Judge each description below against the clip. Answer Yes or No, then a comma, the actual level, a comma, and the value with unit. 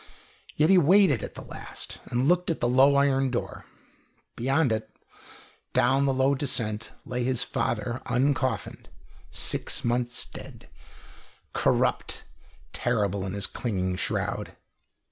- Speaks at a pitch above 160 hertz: No, low, 125 Hz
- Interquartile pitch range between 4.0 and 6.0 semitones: No, average, 3.2 semitones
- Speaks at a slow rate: Yes, slow, 125 wpm